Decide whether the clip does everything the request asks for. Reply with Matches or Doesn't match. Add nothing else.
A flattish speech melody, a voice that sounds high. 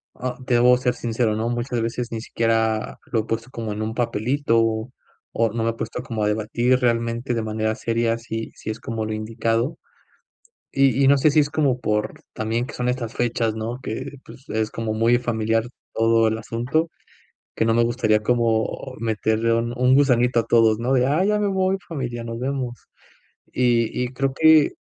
Doesn't match